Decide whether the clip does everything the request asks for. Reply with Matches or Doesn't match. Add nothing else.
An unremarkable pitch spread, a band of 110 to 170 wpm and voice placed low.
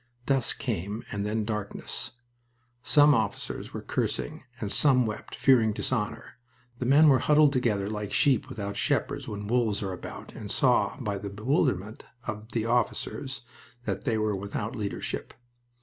Matches